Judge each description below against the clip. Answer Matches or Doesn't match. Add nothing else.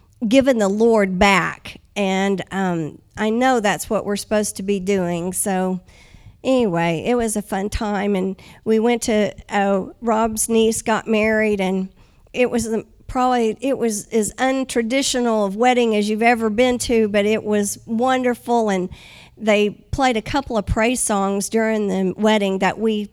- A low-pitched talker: Doesn't match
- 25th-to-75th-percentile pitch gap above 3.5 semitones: Doesn't match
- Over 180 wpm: Doesn't match